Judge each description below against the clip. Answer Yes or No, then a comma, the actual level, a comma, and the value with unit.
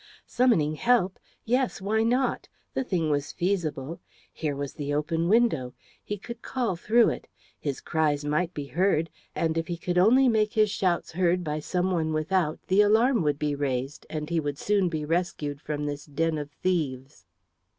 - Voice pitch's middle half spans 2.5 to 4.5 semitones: No, average, 5.2 semitones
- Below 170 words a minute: No, average, 180 wpm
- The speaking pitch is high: No, medium, 165 Hz